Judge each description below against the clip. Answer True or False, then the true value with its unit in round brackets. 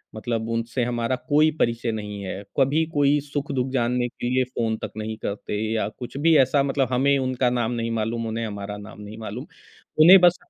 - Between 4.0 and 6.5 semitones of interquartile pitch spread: False (3.4 semitones)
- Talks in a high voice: False (120 Hz)